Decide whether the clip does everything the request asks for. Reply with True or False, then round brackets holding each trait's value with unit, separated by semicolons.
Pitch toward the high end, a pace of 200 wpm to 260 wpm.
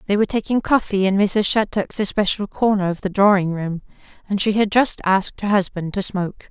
True (200 Hz; 205 wpm)